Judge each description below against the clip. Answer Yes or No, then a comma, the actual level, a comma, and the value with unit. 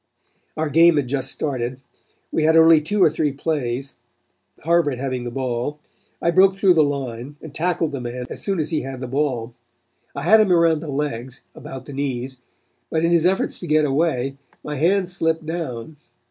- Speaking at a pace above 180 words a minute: Yes, average, 190 wpm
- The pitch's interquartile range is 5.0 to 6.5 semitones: No, average, 4.0 semitones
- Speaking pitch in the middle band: Yes, medium, 150 Hz